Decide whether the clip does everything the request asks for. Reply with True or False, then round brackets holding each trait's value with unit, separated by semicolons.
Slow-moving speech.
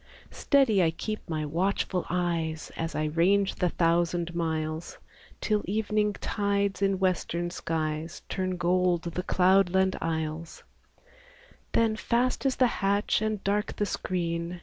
True (130 wpm)